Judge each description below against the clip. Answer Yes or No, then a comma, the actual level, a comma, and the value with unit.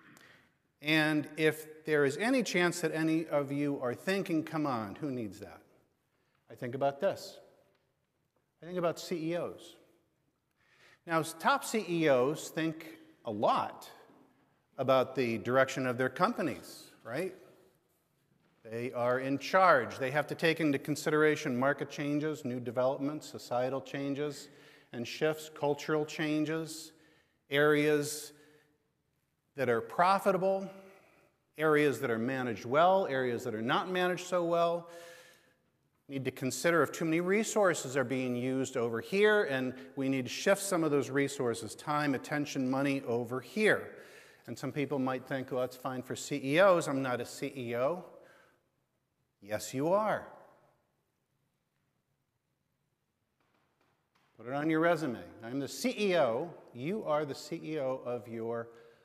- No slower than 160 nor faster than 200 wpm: No, slow, 135 wpm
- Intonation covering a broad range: No, average, 4.0 semitones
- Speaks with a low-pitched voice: No, medium, 150 Hz